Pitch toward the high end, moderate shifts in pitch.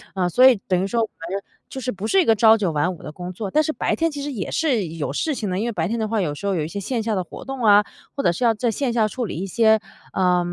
Yes: high, 215 Hz; average, 4.8 semitones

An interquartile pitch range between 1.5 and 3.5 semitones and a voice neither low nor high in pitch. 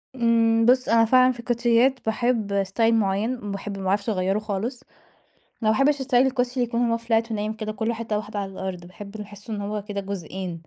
No: average, 2.9 semitones; high, 220 Hz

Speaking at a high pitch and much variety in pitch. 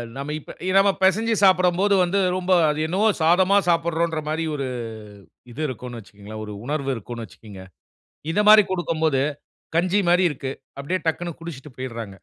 No: medium, 160 Hz; wide, 5.9 semitones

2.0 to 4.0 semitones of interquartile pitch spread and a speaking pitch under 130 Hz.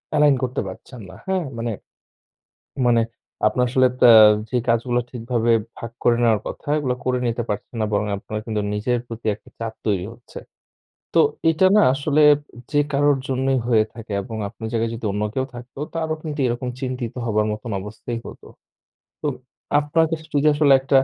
Yes: average, 3.5 semitones; low, 120 Hz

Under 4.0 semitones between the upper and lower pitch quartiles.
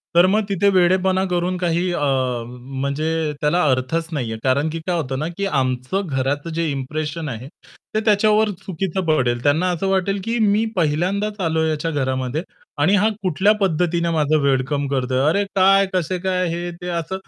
No: average, 5.0 semitones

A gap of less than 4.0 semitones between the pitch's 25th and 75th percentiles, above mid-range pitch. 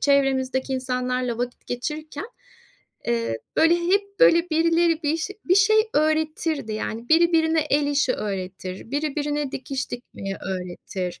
No: average, 4.8 semitones; very high, 285 Hz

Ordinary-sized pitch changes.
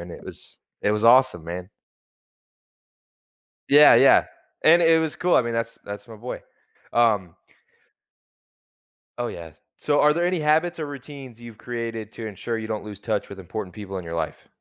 No: wide, 5.9 semitones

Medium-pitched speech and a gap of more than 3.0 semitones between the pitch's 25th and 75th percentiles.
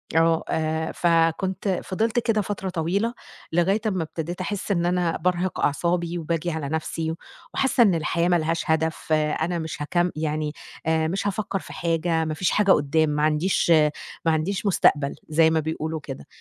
No: medium, 165 Hz; narrow, 2.6 semitones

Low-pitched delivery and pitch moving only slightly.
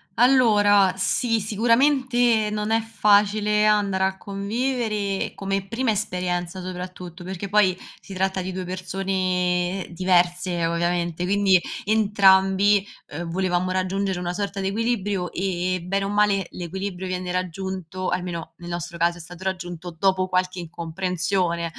No: high, 190 Hz; narrow, 2.3 semitones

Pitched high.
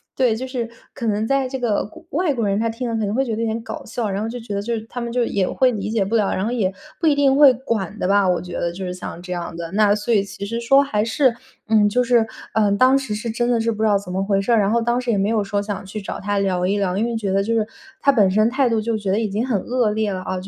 Yes: high, 220 Hz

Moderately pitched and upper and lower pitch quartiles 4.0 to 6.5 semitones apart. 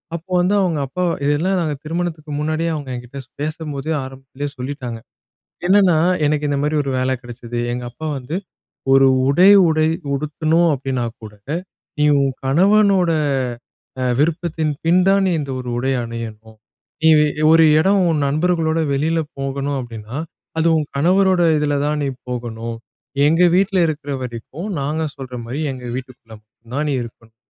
Yes: medium, 145 Hz; average, 4.3 semitones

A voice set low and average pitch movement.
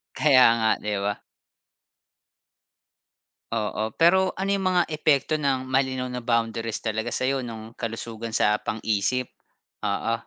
Yes: low, 120 Hz; average, 3.6 semitones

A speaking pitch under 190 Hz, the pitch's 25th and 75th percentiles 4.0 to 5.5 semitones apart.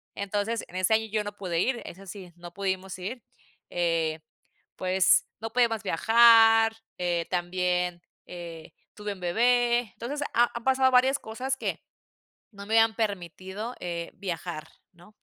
No: high, 200 Hz; average, 4.3 semitones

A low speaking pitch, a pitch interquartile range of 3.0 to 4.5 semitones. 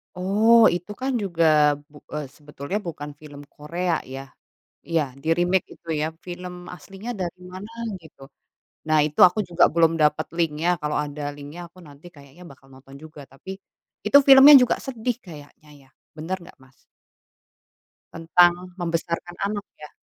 No: medium, 170 Hz; average, 3.5 semitones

